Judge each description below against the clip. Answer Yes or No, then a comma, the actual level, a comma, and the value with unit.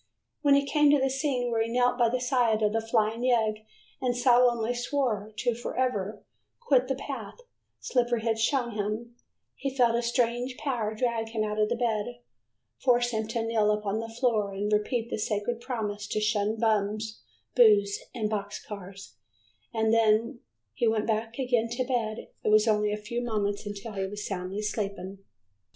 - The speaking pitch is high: Yes, high, 225 Hz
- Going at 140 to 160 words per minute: No, average, 175 wpm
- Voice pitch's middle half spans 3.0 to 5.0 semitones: No, narrow, 2.5 semitones